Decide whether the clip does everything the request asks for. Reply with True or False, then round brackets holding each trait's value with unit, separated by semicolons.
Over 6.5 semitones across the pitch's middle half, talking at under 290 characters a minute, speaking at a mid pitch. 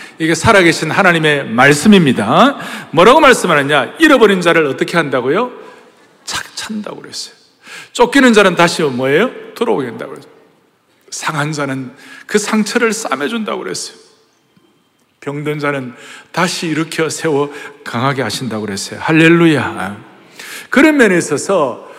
False (7.2 semitones; 310 characters per minute; 165 Hz)